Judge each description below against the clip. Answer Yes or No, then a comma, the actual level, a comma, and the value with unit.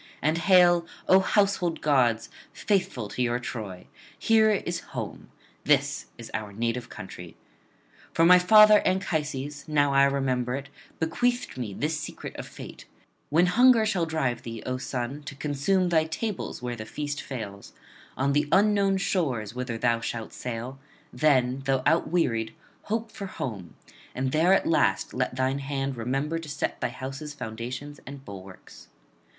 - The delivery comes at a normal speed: Yes, average, 155 wpm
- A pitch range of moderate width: No, wide, 5.9 semitones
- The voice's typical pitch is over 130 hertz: Yes, medium, 140 Hz